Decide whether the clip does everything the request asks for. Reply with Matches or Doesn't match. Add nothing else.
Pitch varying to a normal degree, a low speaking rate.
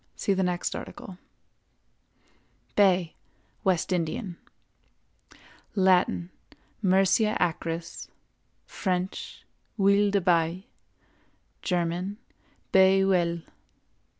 Doesn't match